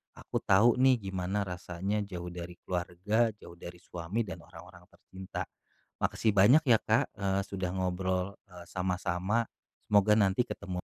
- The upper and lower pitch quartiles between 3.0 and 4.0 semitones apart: No, narrow, 2.6 semitones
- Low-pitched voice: Yes, very low, 95 Hz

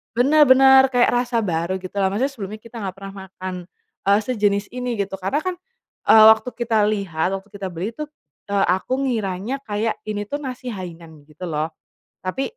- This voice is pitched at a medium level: No, high, 205 Hz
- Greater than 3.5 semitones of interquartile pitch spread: Yes, average, 4.7 semitones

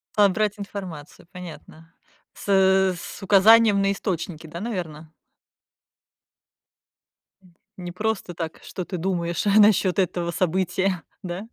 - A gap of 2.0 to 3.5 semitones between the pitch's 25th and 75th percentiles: Yes, average, 2.7 semitones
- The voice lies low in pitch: No, medium, 185 Hz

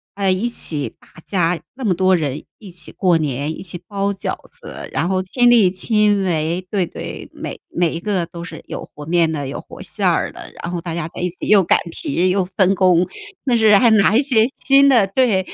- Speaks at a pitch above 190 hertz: No, medium, 185 Hz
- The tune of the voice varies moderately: Yes, average, 3.7 semitones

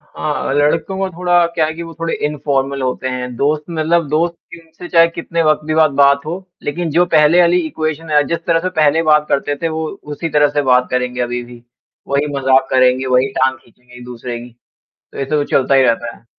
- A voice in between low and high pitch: Yes, medium, 150 Hz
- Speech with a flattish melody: No, average, 4.0 semitones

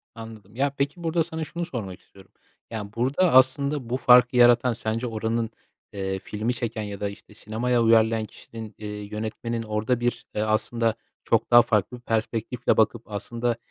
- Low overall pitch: Yes, low, 115 Hz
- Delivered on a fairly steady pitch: Yes, narrow, 2.3 semitones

